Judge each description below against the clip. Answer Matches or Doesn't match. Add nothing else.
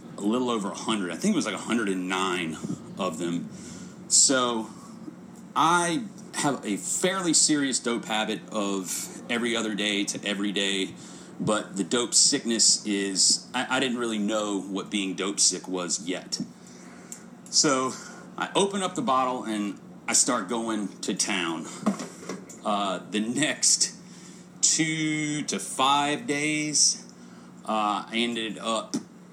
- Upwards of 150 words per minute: Doesn't match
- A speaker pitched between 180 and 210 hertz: Doesn't match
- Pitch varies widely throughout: Matches